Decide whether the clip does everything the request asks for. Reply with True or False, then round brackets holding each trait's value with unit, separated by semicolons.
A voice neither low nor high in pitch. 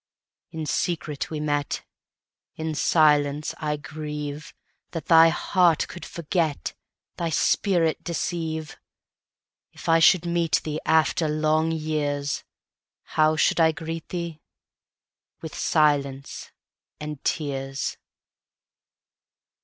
True (155 Hz)